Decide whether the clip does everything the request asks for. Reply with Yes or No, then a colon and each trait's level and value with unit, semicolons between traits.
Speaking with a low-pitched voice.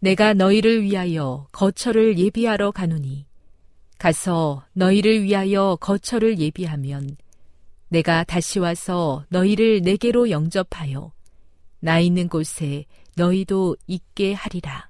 No: medium, 175 Hz